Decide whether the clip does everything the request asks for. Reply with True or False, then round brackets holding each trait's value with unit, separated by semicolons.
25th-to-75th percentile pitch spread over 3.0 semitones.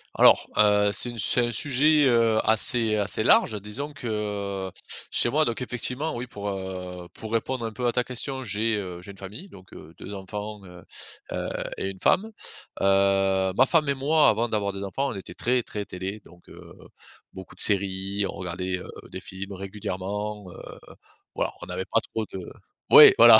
True (3.6 semitones)